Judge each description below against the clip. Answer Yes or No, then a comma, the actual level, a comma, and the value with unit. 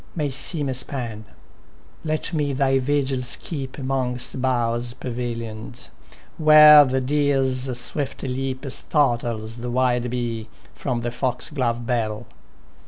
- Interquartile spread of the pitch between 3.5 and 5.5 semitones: No, narrow, 2.4 semitones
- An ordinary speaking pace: No, slow, 115 wpm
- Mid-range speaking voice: No, low, 130 Hz